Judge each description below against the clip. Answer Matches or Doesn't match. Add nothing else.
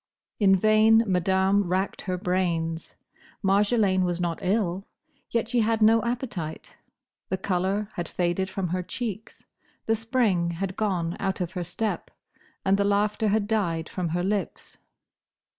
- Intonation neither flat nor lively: Matches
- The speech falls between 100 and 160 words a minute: Matches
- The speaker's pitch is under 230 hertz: Matches